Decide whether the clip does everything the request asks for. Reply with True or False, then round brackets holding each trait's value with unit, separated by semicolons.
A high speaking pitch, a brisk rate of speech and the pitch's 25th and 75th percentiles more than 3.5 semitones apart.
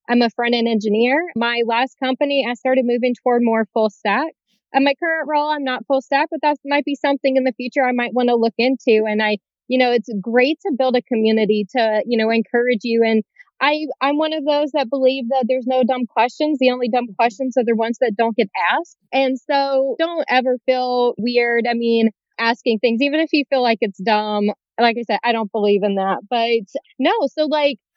False (250 Hz; 225 wpm; 3.0 semitones)